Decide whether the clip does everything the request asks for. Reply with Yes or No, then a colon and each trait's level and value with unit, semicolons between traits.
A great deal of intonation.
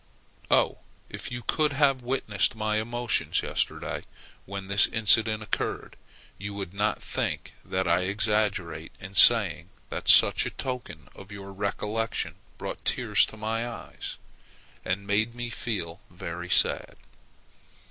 No: average, 2.8 semitones